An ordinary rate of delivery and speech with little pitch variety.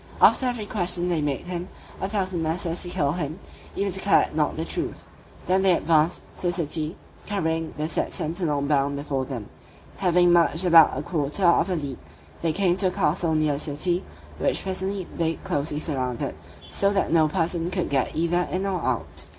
No: average, 190 wpm; average, 3.4 semitones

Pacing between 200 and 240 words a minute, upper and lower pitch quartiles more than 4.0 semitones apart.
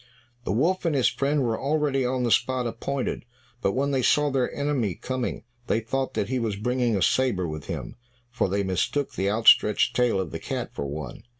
Yes: fast, 205 wpm; average, 5.1 semitones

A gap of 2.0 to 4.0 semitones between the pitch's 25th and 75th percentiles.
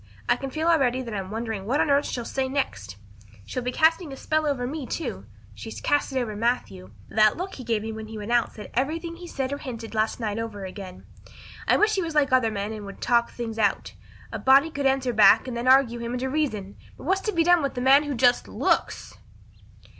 No: average, 4.6 semitones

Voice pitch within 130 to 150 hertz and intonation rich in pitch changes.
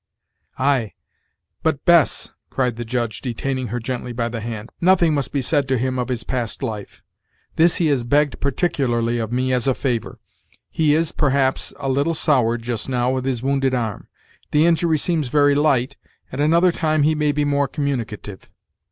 No: low, 135 Hz; average, 3.5 semitones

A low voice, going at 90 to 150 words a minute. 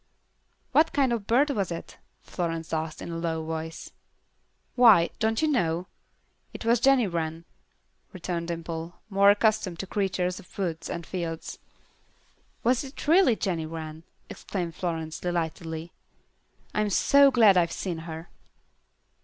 No: medium, 175 Hz; slow, 135 wpm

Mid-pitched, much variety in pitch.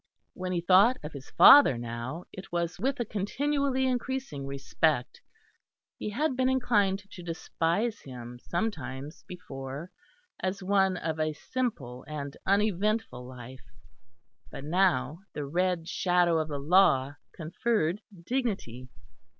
Yes: medium, 175 Hz; wide, 6.9 semitones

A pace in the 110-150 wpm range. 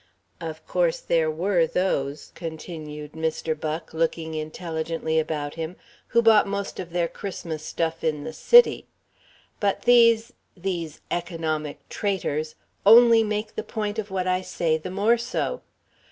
Yes: average, 140 wpm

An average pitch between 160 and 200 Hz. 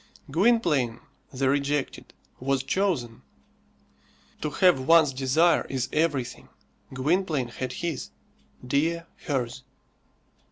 No: medium, 140 Hz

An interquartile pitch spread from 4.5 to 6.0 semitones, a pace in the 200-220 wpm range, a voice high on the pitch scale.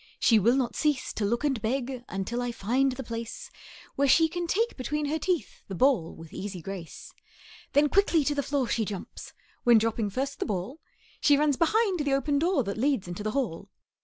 Yes: average, 5.1 semitones; fast, 205 wpm; very high, 260 Hz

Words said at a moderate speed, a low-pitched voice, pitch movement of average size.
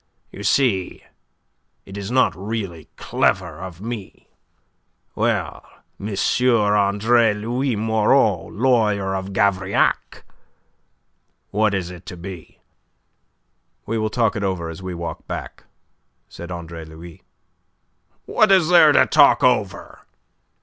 No: slow, 115 wpm; low, 100 Hz; average, 3.7 semitones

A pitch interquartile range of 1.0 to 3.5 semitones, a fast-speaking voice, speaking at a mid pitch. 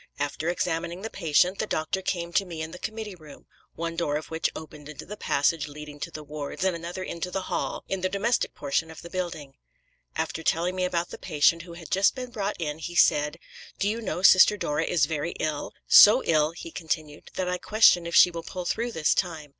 Yes: average, 3.2 semitones; fast, 225 wpm; medium, 170 Hz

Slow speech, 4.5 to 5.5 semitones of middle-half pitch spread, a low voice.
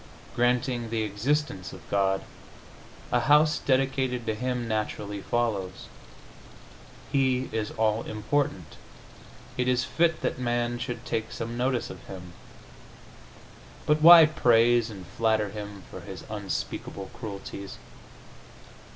No: slow, 115 wpm; average, 3.6 semitones; low, 120 Hz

